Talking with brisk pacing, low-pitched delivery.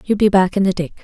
No: fast, 350 wpm; high, 195 Hz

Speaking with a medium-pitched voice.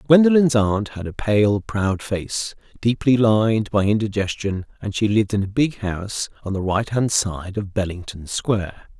No: low, 105 Hz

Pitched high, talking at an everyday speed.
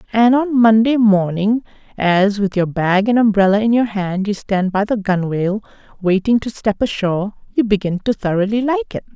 Yes: high, 210 Hz; average, 185 wpm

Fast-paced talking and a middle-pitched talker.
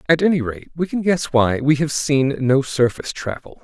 Yes: fast, 215 wpm; medium, 145 Hz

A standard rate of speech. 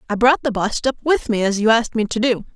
No: fast, 305 wpm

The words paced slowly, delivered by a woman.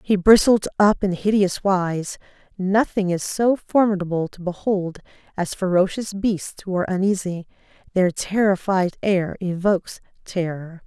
Yes: slow, 125 wpm; female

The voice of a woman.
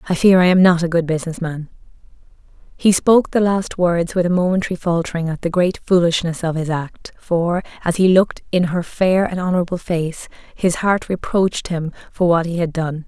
Yes: female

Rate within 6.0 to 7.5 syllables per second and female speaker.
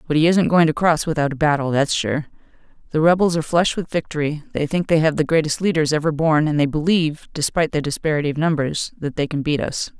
Yes: 6.4 syllables/s; female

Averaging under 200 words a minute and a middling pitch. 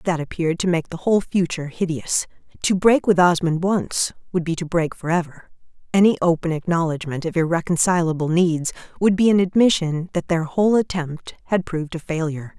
Yes: average, 175 wpm; medium, 170 Hz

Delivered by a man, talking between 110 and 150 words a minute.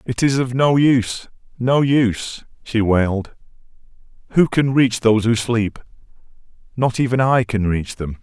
Yes: male; average, 145 wpm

